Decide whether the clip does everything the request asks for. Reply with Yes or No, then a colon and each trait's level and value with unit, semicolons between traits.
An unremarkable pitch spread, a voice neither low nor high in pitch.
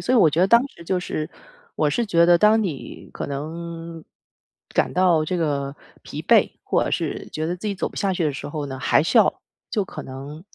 Yes: average, 3.7 semitones; medium, 170 Hz